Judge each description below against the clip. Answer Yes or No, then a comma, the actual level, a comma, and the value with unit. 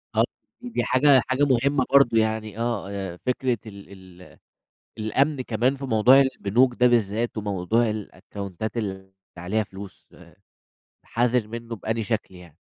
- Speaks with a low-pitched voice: Yes, low, 110 Hz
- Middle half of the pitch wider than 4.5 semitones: No, average, 3.9 semitones